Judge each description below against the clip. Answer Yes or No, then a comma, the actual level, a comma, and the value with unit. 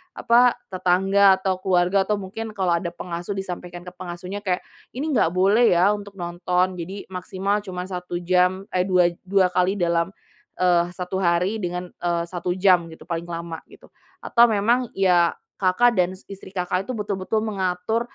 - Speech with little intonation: Yes, narrow, 2.0 semitones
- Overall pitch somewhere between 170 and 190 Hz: Yes, medium, 185 Hz